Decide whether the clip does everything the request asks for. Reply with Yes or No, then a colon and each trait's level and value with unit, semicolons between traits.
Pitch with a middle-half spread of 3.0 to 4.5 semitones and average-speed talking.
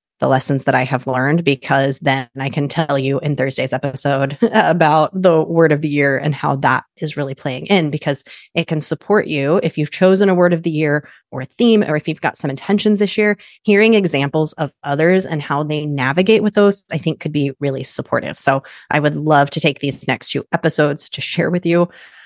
No: average, 3.6 semitones; fast, 220 wpm